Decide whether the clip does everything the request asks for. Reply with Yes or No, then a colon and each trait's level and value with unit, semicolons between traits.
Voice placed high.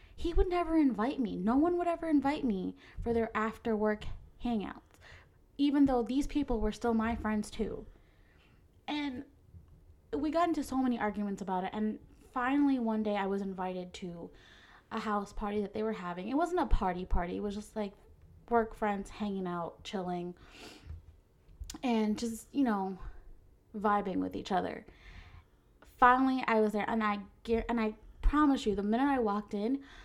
Yes: high, 215 Hz